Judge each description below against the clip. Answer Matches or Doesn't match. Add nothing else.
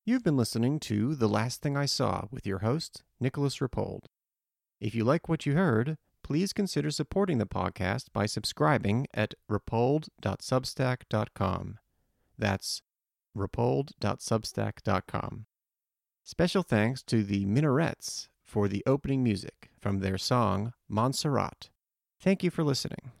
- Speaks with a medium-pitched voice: Doesn't match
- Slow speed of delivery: Matches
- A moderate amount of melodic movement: Doesn't match